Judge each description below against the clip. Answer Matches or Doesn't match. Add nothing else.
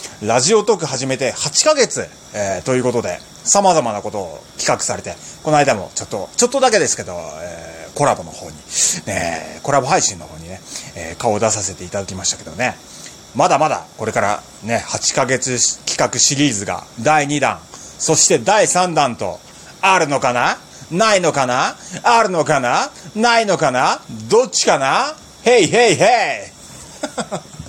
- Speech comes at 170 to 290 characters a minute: Doesn't match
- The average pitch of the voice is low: Matches